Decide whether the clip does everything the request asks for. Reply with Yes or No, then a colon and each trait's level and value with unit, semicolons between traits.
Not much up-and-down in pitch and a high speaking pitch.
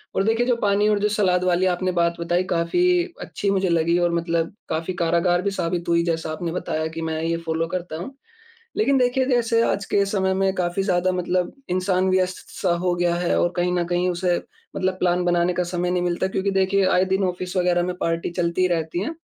No: narrow, 1.8 semitones; medium, 180 Hz